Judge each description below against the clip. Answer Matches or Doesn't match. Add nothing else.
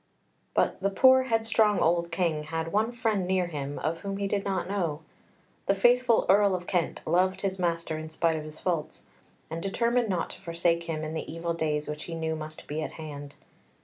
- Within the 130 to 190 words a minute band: Doesn't match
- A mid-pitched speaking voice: Matches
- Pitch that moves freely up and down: Doesn't match